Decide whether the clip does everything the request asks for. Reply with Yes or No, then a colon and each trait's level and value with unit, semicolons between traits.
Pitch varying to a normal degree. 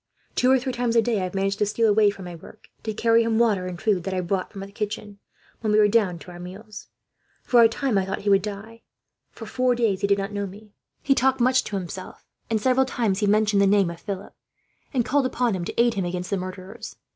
Yes: average, 3.1 semitones